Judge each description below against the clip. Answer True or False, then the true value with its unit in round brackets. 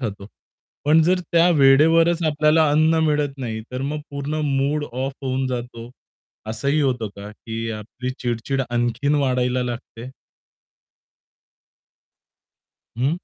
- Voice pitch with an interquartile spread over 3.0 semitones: True (3.8 semitones)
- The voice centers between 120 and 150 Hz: True (135 Hz)